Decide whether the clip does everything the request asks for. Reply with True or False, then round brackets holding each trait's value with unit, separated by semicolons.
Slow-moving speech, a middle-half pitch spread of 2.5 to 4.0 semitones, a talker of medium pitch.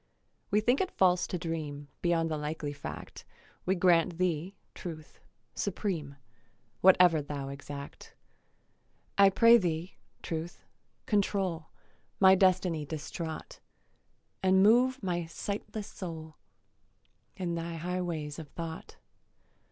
True (115 wpm; 3.1 semitones; 170 Hz)